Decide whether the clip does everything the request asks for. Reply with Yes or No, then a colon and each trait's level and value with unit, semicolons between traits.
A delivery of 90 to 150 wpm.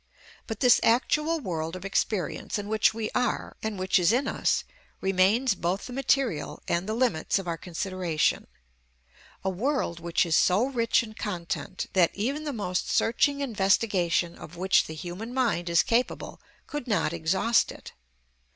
No: average, 160 wpm